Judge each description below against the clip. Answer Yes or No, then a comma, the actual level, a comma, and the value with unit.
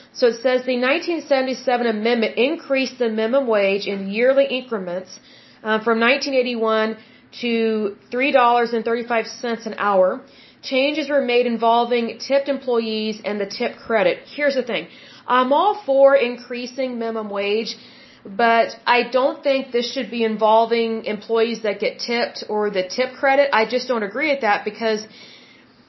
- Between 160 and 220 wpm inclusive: No, average, 145 wpm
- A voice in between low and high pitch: No, high, 240 Hz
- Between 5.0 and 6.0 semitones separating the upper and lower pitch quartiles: No, average, 2.9 semitones